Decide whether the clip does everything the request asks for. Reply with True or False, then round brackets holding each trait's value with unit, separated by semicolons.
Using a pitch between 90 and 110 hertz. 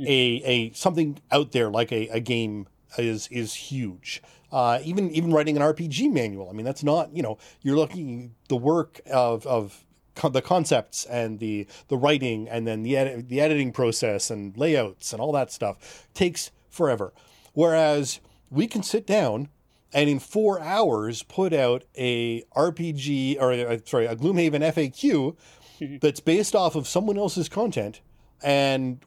False (140 Hz)